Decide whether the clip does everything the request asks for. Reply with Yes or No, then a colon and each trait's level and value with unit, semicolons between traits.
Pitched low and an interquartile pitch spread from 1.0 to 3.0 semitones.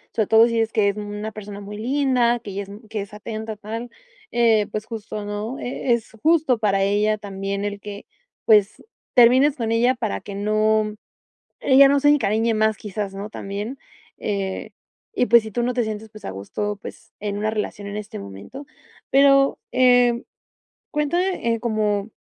No: high, 215 Hz; average, 2.7 semitones